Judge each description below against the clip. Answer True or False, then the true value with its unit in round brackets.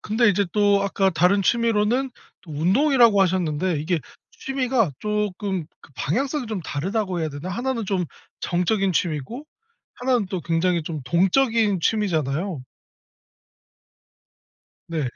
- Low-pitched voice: False (195 Hz)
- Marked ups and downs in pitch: False (4.8 semitones)